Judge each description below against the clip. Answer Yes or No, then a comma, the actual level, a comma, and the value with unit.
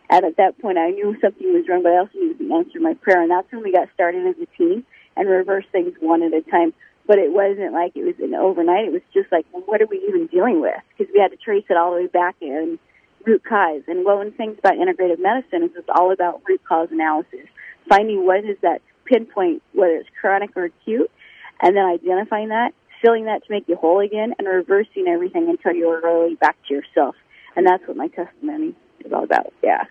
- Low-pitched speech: No, high, 200 Hz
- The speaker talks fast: Yes, fast, 240 wpm